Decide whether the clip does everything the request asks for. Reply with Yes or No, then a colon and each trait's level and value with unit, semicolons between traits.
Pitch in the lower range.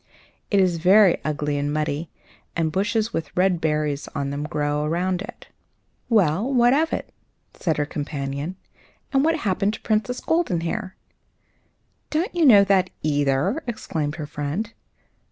No: medium, 175 Hz